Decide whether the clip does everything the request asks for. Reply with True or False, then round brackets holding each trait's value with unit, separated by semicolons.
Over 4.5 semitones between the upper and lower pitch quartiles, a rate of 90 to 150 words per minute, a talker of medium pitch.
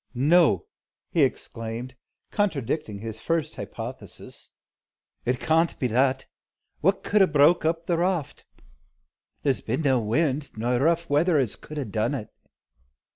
True (5.2 semitones; 140 wpm; 145 Hz)